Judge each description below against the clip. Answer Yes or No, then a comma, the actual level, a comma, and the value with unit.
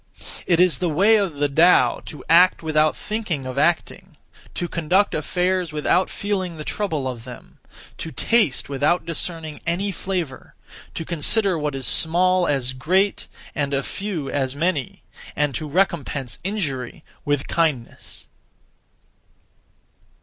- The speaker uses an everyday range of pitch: Yes, average, 4.3 semitones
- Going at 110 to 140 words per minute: Yes, slow, 135 wpm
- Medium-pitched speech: Yes, medium, 165 Hz